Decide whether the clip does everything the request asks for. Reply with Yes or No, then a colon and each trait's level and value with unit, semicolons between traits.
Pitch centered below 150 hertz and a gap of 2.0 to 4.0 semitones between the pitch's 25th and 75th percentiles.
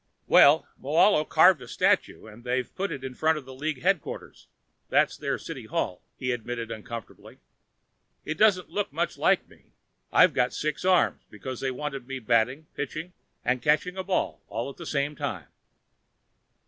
No: medium, 140 Hz; average, 4.4 semitones